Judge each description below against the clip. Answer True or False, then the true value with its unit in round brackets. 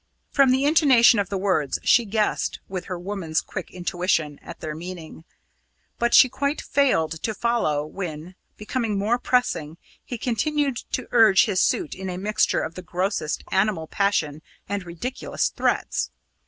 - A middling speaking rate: True (155 wpm)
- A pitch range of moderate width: False (5.8 semitones)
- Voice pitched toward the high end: True (195 Hz)